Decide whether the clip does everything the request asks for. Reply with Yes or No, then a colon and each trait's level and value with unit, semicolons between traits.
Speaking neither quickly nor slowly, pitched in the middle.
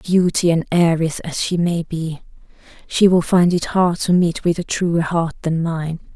Yes: average, 195 wpm; medium, 170 Hz